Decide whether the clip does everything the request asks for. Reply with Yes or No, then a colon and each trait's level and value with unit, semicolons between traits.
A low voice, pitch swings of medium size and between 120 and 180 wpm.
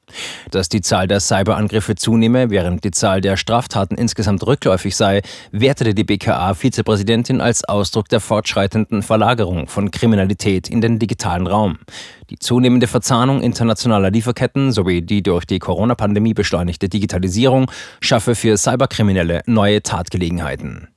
Yes: low, 110 Hz; average, 3.0 semitones; average, 130 wpm